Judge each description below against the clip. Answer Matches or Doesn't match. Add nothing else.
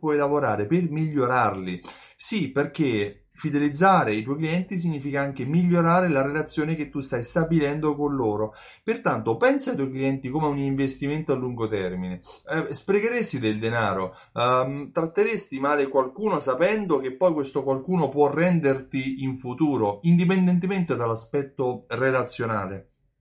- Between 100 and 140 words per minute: Matches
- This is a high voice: Doesn't match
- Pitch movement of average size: Matches